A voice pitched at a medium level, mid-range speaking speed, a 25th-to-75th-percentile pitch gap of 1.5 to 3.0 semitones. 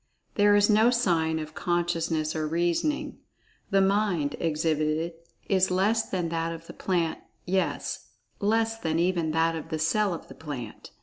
No: medium, 170 Hz; average, 150 wpm; average, 3.5 semitones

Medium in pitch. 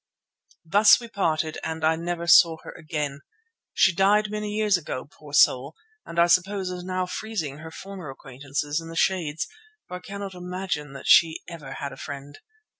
Yes: medium, 170 Hz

